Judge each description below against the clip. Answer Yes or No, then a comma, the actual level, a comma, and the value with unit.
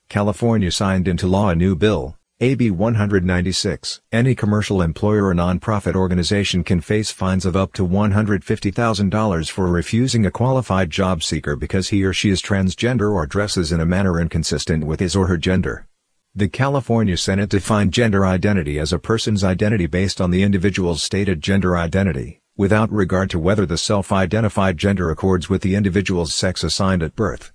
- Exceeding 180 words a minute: No, average, 170 wpm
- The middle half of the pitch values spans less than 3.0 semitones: Yes, narrow, 2.5 semitones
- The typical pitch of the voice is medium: No, very low, 95 Hz